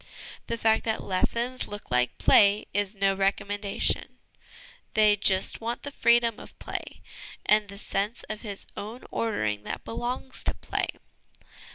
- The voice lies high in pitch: Yes, high, 210 Hz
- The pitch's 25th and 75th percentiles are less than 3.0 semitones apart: Yes, narrow, 2.6 semitones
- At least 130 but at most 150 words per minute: Yes, average, 145 wpm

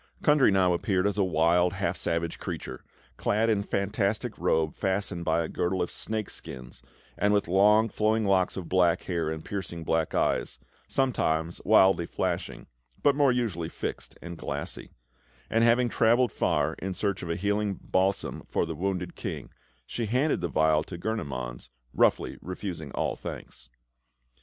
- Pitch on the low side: Yes, very low, 95 Hz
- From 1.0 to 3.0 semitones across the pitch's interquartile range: No, average, 4.0 semitones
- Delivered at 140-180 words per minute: Yes, average, 160 wpm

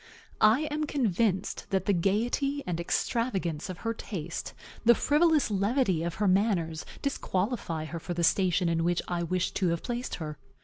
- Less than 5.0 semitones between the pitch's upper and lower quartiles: No, wide, 5.5 semitones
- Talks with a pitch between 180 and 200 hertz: Yes, high, 190 Hz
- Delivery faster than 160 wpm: Yes, average, 170 wpm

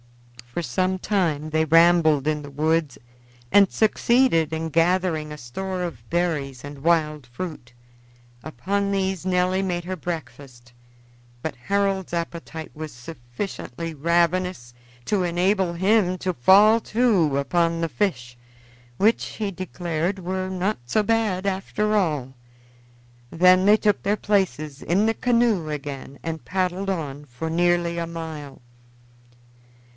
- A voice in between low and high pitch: Yes, medium, 170 Hz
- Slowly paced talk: Yes, slow, 130 wpm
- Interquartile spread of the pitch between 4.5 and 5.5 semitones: No, average, 3.9 semitones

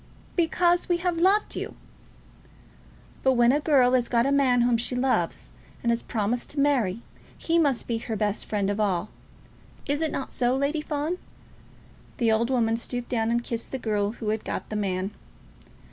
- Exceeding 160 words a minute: Yes, average, 185 wpm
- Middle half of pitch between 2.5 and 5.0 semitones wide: Yes, average, 4.3 semitones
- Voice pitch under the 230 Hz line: No, high, 245 Hz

